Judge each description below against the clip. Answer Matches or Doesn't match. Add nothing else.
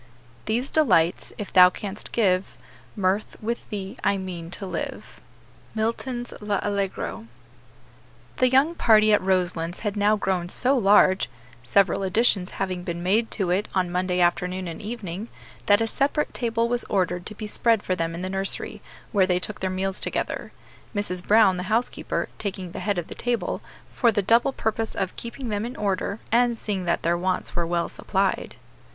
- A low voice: Doesn't match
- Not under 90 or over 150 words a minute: Doesn't match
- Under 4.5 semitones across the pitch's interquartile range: Matches